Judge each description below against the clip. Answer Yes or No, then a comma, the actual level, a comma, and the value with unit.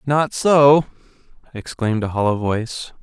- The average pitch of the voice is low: Yes, low, 125 Hz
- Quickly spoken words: No, slow, 120 wpm